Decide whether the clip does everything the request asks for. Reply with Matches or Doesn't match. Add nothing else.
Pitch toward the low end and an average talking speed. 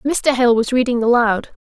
Doesn't match